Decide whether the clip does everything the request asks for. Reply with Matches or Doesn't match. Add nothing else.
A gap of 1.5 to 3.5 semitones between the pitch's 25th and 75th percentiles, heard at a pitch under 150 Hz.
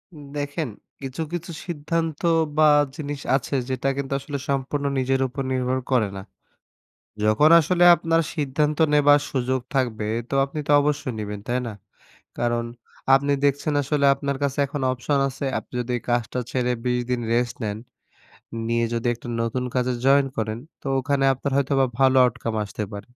Matches